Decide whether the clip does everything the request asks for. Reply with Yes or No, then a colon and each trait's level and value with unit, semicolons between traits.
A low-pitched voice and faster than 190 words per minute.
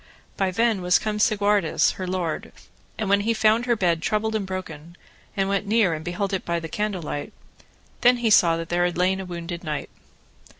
No: high, 190 Hz; average, 200 wpm